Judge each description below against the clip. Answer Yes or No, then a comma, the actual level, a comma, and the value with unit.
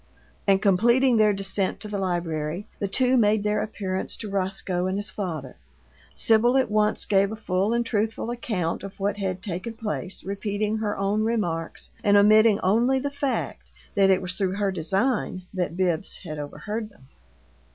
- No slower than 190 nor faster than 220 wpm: No, average, 170 wpm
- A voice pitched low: No, high, 200 Hz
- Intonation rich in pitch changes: No, average, 2.7 semitones